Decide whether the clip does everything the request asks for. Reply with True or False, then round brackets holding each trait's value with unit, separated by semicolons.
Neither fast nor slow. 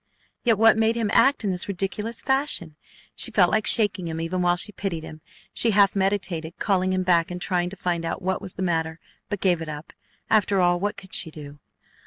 False (220 wpm)